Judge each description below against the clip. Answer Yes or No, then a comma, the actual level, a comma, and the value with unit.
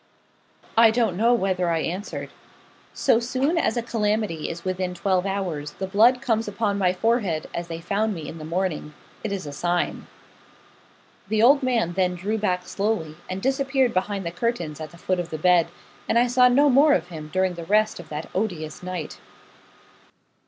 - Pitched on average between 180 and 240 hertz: Yes, high, 190 Hz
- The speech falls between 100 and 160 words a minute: No, average, 190 wpm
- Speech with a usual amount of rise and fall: Yes, average, 4.7 semitones